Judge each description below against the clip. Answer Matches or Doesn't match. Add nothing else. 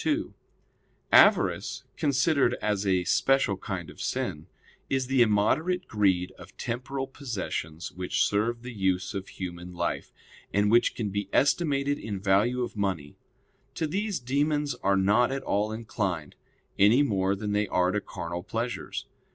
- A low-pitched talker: Matches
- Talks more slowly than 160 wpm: Matches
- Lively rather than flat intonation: Matches